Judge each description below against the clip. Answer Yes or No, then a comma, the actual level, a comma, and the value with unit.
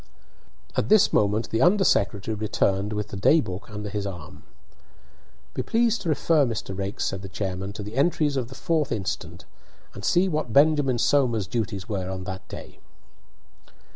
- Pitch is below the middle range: Yes, low, 110 Hz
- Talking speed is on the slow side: No, average, 170 wpm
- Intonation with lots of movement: Yes, wide, 6.9 semitones